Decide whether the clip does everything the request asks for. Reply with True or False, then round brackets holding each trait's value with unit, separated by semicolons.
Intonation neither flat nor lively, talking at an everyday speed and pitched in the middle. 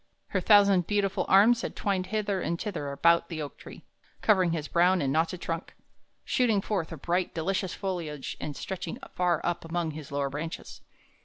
True (3.3 semitones; 175 wpm; 175 Hz)